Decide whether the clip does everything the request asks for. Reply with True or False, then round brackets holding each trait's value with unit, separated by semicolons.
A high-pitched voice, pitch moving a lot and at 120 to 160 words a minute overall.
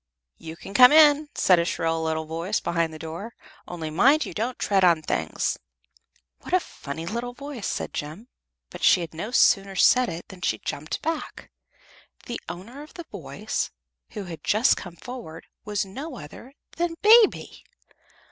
False (195 Hz; 7.7 semitones; 170 wpm)